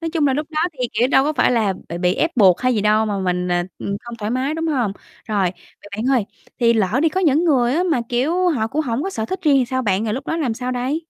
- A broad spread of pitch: Yes, wide, 6.0 semitones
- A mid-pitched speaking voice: No, very high, 250 Hz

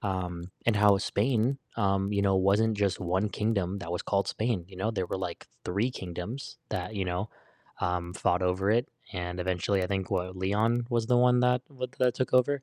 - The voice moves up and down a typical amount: Yes, average, 3.7 semitones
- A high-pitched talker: No, low, 100 Hz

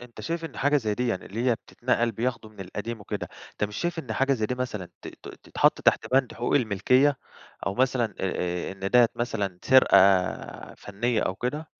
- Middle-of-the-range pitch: No, low, 120 Hz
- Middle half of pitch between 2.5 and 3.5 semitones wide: No, average, 4.0 semitones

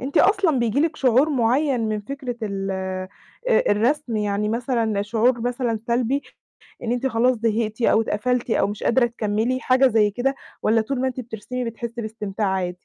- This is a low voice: No, high, 235 Hz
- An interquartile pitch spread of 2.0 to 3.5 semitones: Yes, average, 3.1 semitones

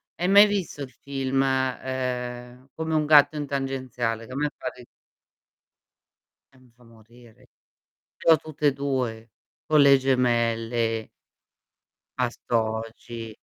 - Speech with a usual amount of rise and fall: Yes, average, 3.1 semitones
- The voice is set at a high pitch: No, low, 130 Hz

